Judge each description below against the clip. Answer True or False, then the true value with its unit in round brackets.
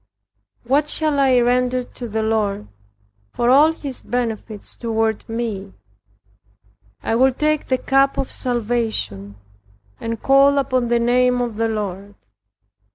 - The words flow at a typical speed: False (130 wpm)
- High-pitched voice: True (240 Hz)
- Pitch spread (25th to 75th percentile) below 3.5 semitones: True (2.9 semitones)